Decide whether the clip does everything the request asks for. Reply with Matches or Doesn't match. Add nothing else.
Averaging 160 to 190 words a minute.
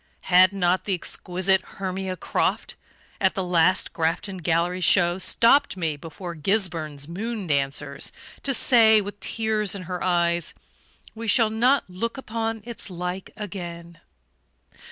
Doesn't match